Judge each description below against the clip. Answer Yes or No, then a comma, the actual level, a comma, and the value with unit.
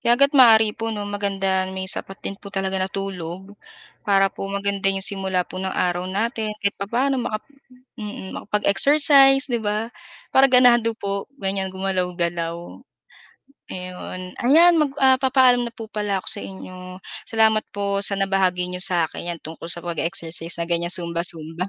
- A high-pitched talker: Yes, high, 195 Hz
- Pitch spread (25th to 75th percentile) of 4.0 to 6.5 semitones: No, average, 3.4 semitones